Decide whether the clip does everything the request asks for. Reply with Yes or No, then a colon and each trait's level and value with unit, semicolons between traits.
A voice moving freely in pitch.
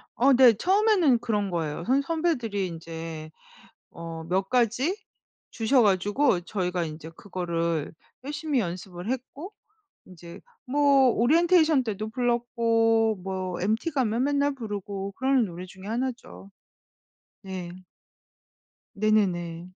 Yes: wide, 6.4 semitones